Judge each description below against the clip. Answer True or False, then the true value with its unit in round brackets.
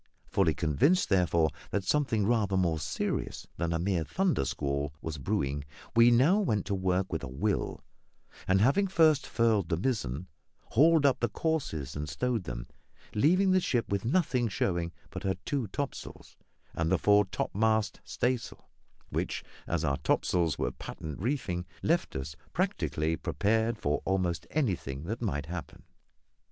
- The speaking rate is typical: True (155 wpm)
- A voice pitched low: True (95 Hz)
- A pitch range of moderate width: False (6.9 semitones)